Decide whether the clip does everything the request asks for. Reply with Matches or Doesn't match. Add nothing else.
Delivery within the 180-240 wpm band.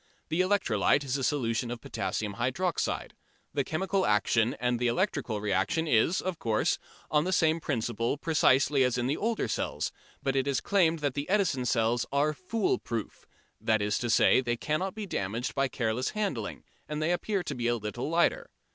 Matches